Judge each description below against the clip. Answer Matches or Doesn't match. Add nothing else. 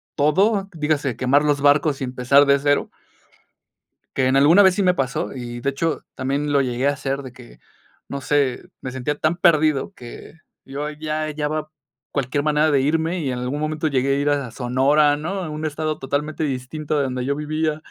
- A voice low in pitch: Doesn't match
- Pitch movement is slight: Matches